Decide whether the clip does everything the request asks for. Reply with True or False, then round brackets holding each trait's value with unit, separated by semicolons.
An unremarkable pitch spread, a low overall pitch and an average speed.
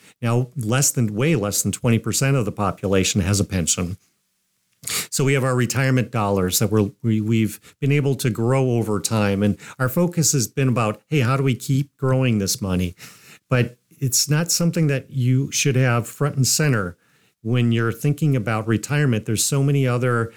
True (4.3 semitones; 120 Hz; 190 wpm)